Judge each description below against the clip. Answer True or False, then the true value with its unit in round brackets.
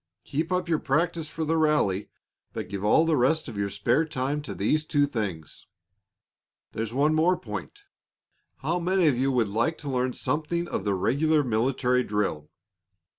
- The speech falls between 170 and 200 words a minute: True (175 wpm)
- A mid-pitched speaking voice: True (145 Hz)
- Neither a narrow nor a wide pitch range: False (6.1 semitones)